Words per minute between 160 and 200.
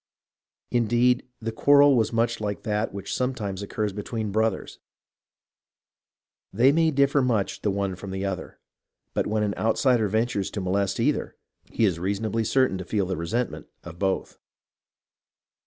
No: average, 150 wpm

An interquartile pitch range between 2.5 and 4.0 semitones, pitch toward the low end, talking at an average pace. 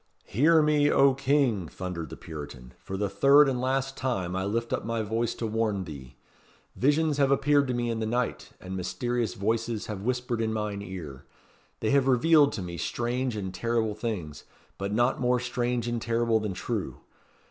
No: average, 4.6 semitones; low, 115 Hz; average, 185 wpm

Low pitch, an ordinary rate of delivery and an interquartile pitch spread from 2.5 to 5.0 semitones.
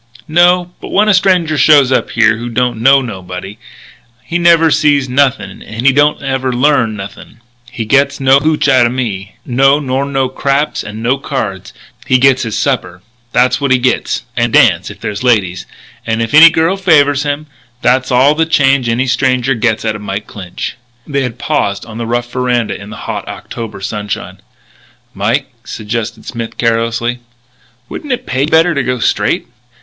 Yes: low, 130 Hz; average, 180 wpm; average, 3.8 semitones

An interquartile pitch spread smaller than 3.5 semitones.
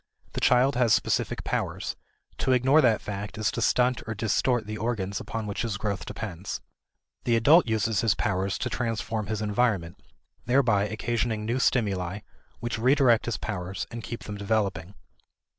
Yes: average, 3.0 semitones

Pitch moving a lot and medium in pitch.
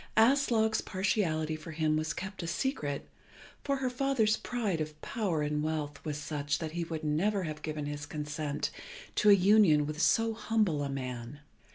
Yes: wide, 6.1 semitones; medium, 160 Hz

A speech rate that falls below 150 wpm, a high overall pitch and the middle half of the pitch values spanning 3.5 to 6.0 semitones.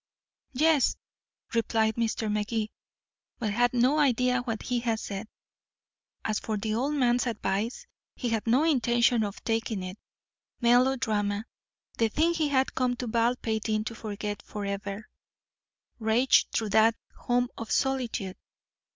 No: slow, 135 wpm; high, 230 Hz; narrow, 2.6 semitones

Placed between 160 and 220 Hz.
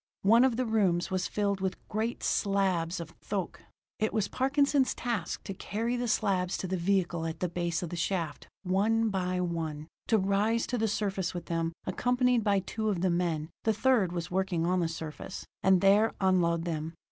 Yes: high, 190 Hz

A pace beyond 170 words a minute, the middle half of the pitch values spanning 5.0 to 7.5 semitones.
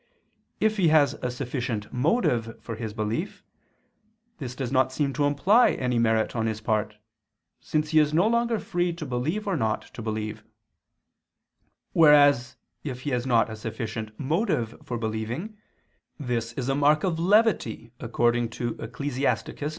No: average, 155 wpm; wide, 5.4 semitones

